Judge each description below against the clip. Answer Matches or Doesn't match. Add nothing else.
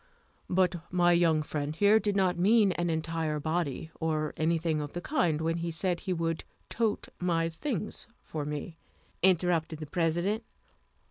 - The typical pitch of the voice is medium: Matches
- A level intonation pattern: Matches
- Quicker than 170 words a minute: Doesn't match